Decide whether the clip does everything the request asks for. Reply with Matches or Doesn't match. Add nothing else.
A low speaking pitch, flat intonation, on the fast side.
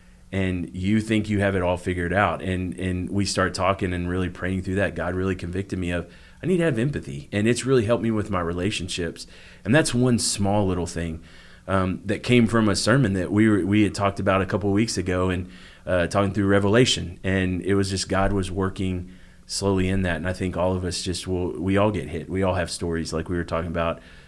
Matches